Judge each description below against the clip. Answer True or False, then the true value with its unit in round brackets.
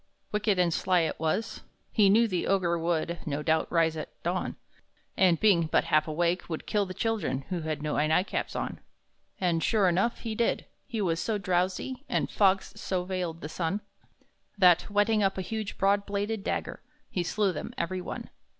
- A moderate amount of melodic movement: True (3.5 semitones)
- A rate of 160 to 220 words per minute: True (185 wpm)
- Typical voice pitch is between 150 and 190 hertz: True (185 Hz)